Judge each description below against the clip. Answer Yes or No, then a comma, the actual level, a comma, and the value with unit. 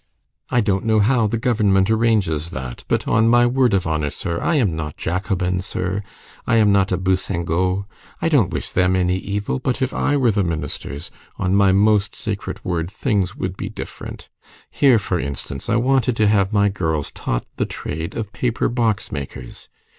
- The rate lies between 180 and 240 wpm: Yes, average, 185 wpm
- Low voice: Yes, low, 100 Hz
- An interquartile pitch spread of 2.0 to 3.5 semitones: No, average, 4.1 semitones